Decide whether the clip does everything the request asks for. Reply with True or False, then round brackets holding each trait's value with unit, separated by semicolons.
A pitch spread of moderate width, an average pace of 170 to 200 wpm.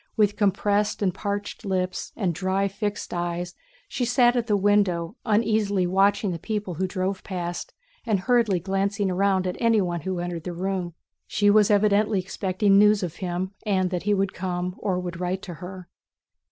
False (2.3 semitones; 175 wpm)